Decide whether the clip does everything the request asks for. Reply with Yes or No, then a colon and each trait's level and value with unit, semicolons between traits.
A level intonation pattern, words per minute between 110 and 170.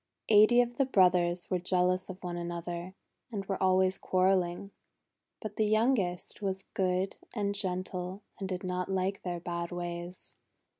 Yes: narrow, 1.8 semitones; average, 155 wpm